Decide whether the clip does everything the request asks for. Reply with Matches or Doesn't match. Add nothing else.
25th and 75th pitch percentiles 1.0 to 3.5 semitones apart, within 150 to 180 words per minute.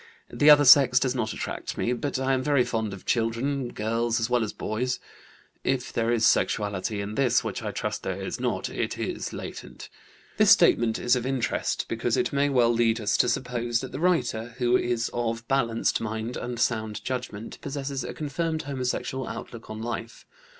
Doesn't match